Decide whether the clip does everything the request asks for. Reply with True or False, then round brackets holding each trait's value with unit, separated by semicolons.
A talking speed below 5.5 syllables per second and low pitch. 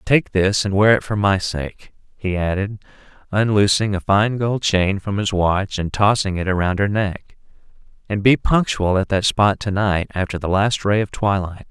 True (4.5 syllables/s; 100 Hz)